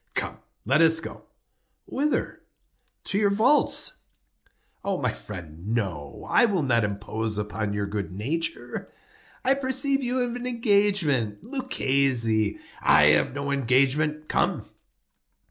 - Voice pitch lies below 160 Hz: Yes, medium, 140 Hz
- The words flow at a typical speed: No, slow, 115 wpm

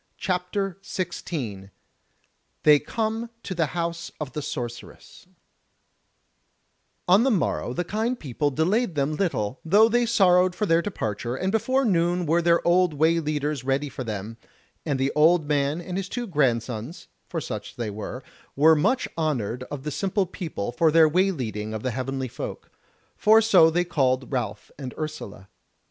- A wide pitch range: Yes, wide, 5.9 semitones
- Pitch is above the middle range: No, medium, 155 Hz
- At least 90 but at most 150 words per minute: No, average, 160 wpm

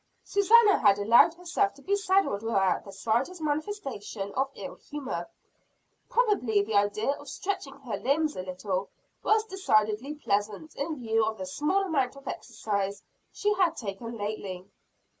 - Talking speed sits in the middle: Yes, average, 150 wpm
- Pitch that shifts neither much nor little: No, wide, 8.6 semitones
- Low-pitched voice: No, very high, 250 Hz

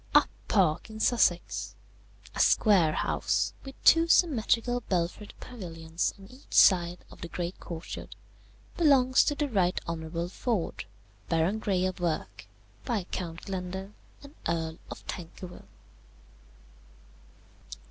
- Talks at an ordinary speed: No, slow, 115 wpm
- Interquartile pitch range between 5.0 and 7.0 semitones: Yes, wide, 5.4 semitones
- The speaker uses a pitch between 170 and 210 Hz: Yes, medium, 185 Hz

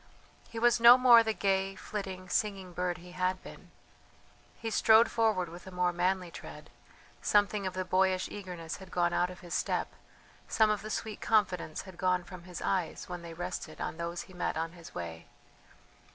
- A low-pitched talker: No, medium, 185 Hz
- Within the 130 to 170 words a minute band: No, average, 190 wpm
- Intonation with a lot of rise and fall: No, narrow, 2.6 semitones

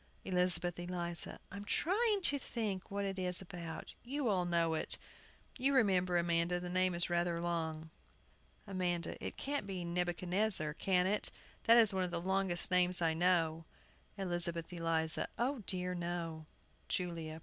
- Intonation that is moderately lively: No, narrow, 2.2 semitones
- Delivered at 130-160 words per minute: Yes, average, 155 wpm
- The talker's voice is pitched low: No, medium, 180 Hz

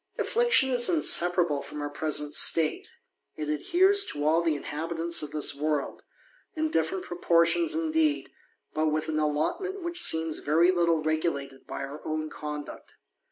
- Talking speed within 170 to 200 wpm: No, average, 150 wpm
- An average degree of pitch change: No, wide, 8.5 semitones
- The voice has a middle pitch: Yes, medium, 160 Hz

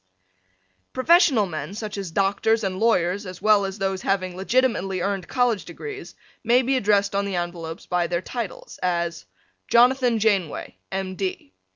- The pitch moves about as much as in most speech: Yes, average, 3.8 semitones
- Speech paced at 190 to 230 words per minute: No, average, 155 wpm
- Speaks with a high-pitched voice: Yes, high, 195 Hz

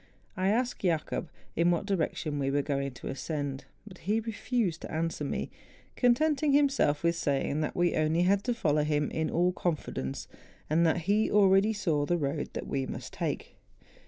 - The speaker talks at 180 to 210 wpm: Yes, average, 185 wpm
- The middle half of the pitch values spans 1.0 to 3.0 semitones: No, wide, 5.4 semitones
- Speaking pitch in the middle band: Yes, medium, 170 Hz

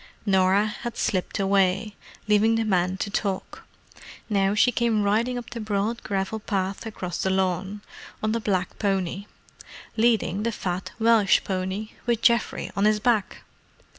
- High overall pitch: Yes, high, 205 Hz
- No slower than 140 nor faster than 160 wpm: Yes, average, 150 wpm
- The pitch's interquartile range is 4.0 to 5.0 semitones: No, narrow, 2.6 semitones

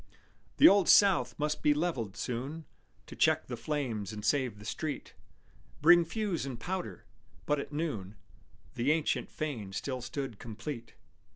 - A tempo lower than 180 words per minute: Yes, average, 150 wpm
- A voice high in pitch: No, medium, 140 Hz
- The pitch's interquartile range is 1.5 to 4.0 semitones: No, wide, 5.5 semitones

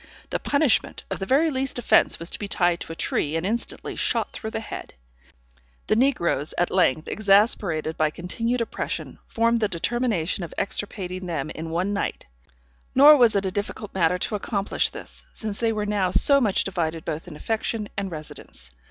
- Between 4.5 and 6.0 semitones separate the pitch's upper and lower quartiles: Yes, average, 4.9 semitones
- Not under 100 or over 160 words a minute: No, average, 185 wpm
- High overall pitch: Yes, high, 200 Hz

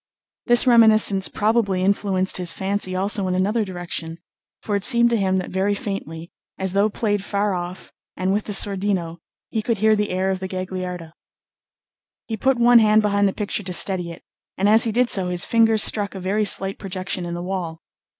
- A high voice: Yes, high, 195 Hz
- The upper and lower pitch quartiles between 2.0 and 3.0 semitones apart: Yes, narrow, 2.5 semitones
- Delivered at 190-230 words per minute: Yes, average, 200 wpm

